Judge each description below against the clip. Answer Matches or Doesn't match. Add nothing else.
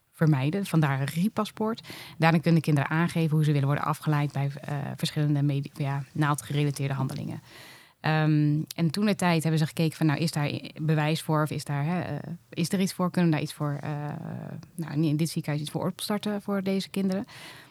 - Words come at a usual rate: Doesn't match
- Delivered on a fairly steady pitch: Matches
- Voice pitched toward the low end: Doesn't match